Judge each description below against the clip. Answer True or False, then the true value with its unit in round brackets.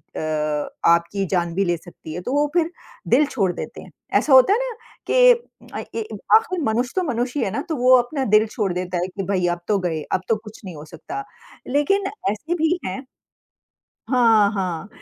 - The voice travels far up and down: True (7.3 semitones)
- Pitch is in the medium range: False (210 Hz)